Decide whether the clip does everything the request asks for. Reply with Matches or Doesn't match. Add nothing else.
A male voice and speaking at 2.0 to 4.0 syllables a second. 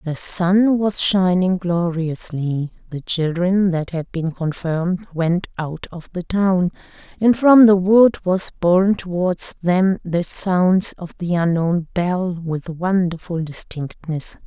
Doesn't match